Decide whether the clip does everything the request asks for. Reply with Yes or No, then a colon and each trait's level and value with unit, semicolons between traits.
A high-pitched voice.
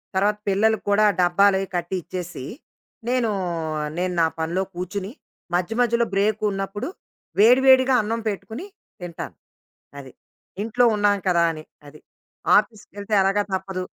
Yes: high, 200 Hz